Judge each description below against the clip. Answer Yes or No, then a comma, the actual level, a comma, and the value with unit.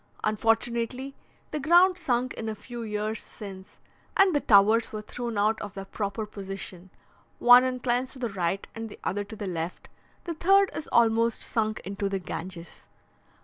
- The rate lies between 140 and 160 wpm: No, average, 170 wpm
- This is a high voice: Yes, high, 220 Hz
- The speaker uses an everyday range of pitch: Yes, average, 3.7 semitones